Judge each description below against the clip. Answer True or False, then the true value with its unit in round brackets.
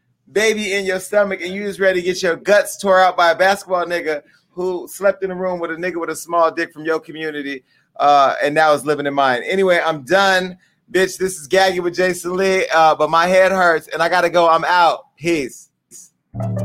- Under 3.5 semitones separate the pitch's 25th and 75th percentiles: True (2.9 semitones)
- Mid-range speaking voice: True (175 Hz)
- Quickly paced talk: True (225 wpm)